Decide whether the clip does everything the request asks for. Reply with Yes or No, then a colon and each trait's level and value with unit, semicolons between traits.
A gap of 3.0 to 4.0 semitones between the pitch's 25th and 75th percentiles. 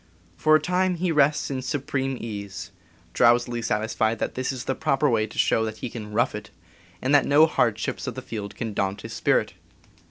No: average, 4.5 semitones